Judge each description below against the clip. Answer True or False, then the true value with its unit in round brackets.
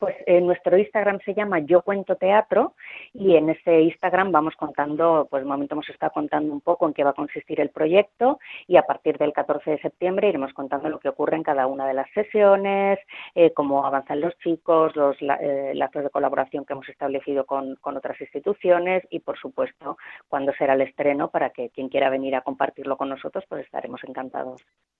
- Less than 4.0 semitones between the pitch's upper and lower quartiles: False (4.3 semitones)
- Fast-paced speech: True (200 wpm)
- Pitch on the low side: False (150 Hz)